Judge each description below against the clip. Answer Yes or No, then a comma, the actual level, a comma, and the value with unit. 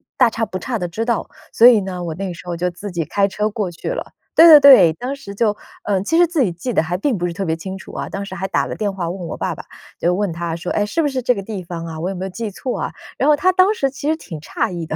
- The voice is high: Yes, high, 195 Hz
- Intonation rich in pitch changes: Yes, wide, 5.8 semitones